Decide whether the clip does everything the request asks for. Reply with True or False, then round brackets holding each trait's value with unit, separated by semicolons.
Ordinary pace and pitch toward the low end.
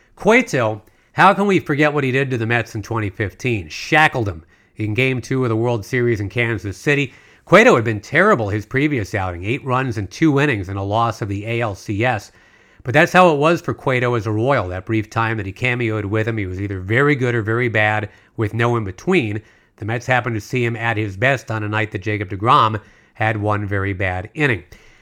False (225 wpm; 115 Hz)